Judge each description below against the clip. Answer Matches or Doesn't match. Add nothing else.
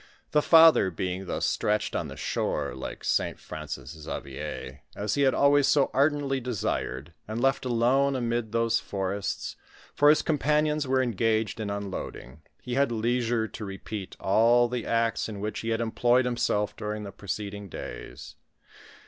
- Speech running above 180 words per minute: Doesn't match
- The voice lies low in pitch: Matches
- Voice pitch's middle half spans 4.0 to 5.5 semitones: Matches